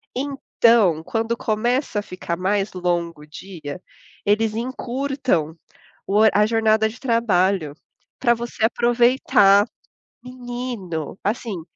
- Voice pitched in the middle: No, high, 215 Hz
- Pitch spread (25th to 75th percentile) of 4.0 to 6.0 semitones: Yes, average, 4.6 semitones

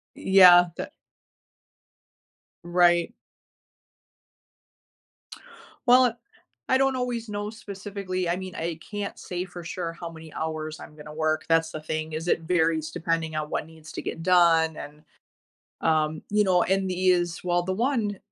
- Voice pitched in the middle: Yes, medium, 175 Hz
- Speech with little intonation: No, average, 3.1 semitones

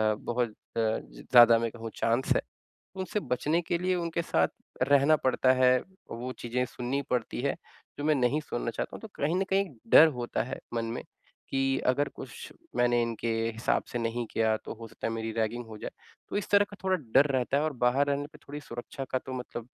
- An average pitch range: Yes, average, 3.7 semitones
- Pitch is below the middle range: Yes, low, 125 Hz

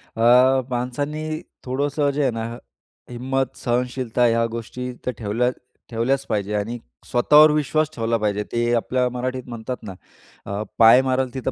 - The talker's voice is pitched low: Yes, low, 125 Hz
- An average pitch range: No, narrow, 2.3 semitones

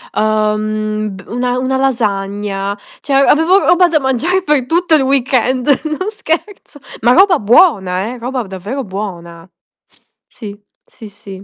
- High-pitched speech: Yes, high, 245 Hz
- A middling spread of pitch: No, wide, 6.3 semitones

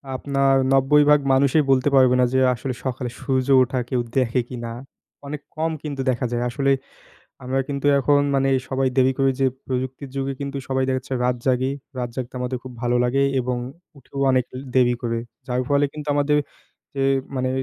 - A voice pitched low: Yes, low, 130 Hz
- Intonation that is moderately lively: No, narrow, 1.6 semitones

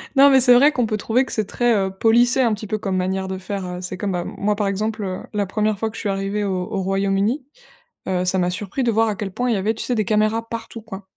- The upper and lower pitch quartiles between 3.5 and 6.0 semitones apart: No, average, 2.9 semitones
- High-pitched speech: Yes, high, 210 Hz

